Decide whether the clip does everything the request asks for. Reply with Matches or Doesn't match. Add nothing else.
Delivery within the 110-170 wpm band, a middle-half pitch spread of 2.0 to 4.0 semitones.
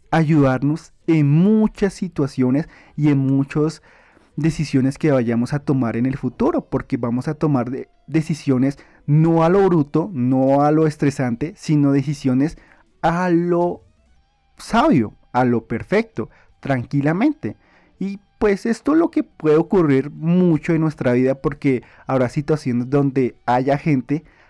Matches